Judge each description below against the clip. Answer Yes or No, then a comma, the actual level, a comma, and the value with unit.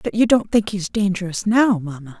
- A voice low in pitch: No, high, 195 Hz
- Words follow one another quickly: Yes, fast, 245 wpm